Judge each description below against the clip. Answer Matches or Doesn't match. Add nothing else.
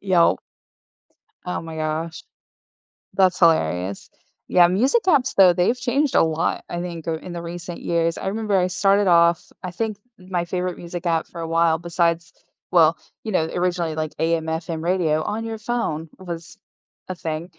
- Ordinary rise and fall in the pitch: Doesn't match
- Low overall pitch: Doesn't match